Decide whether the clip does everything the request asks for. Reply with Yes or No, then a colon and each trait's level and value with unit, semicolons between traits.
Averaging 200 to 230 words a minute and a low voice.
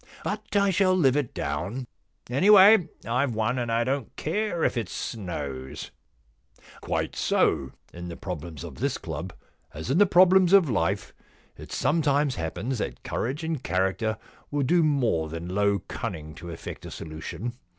No: average, 165 wpm; low, 120 Hz